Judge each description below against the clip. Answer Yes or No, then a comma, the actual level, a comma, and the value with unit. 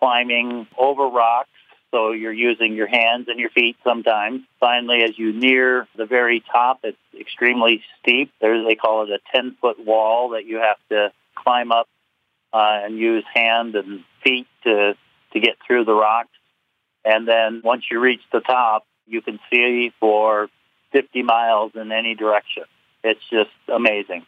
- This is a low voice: Yes, low, 115 Hz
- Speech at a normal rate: Yes, average, 165 wpm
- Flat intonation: Yes, narrow, 1.9 semitones